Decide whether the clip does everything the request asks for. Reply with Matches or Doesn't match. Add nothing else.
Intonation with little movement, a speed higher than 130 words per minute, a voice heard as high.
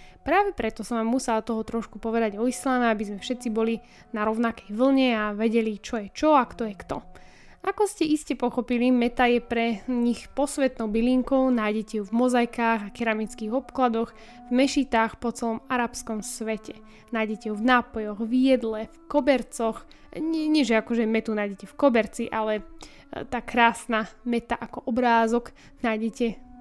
Matches